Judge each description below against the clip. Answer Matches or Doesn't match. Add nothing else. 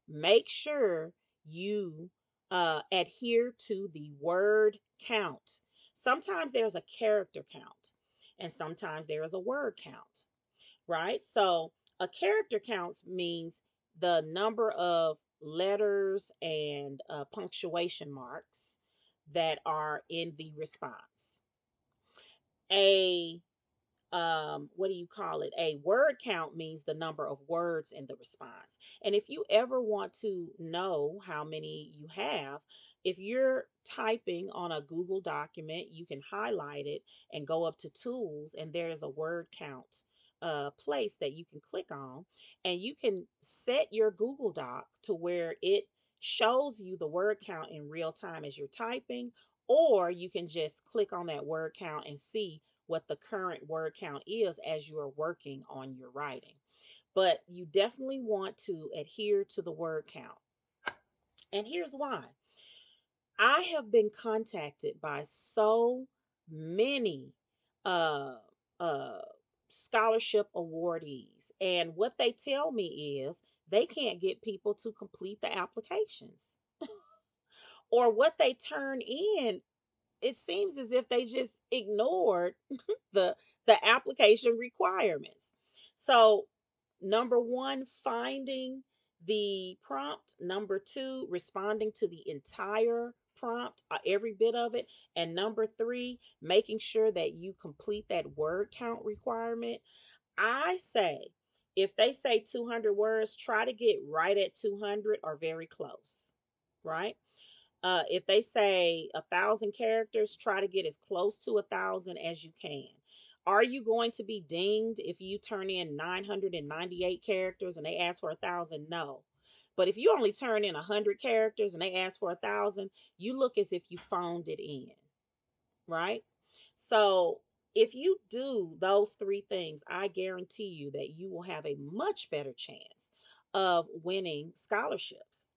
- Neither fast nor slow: Matches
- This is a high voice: Matches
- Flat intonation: Doesn't match